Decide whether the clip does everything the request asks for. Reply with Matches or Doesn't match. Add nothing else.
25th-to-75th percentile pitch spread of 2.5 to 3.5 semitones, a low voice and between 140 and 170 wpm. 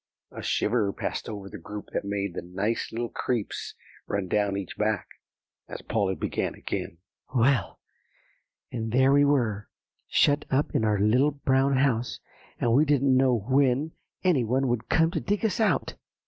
Doesn't match